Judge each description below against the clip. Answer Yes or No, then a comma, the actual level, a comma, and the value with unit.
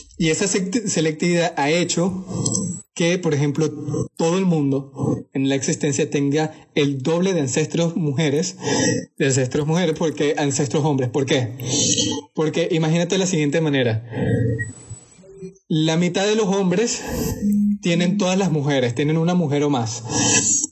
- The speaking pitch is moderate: Yes, medium, 160 Hz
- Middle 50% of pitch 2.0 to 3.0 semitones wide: No, average, 3.6 semitones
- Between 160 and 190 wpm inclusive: No, average, 140 wpm